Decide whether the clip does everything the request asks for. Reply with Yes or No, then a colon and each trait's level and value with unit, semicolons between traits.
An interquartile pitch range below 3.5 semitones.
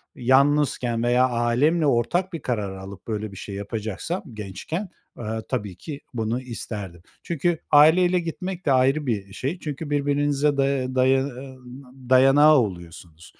No: average, 5.3 semitones